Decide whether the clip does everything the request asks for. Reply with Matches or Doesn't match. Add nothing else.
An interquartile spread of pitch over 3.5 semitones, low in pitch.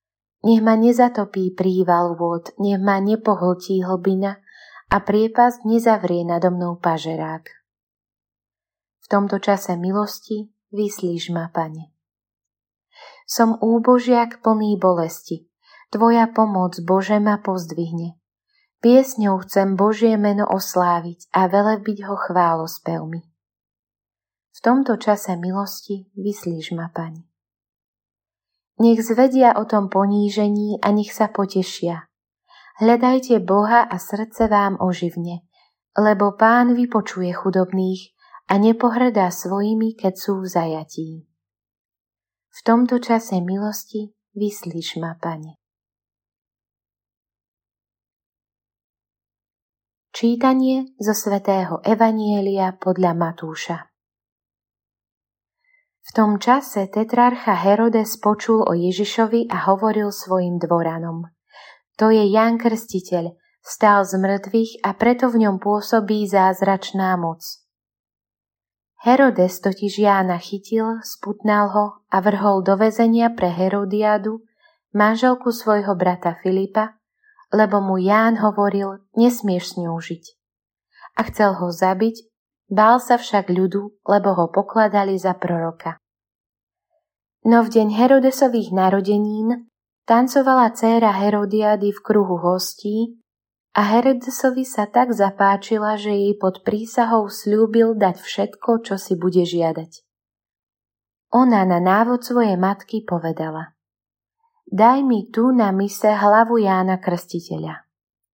Doesn't match